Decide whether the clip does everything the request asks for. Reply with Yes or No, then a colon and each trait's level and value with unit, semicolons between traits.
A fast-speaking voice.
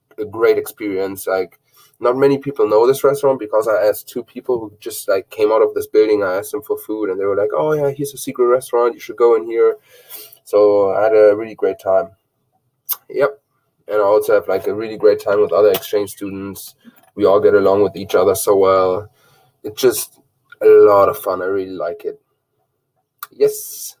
Yes: fast, 210 wpm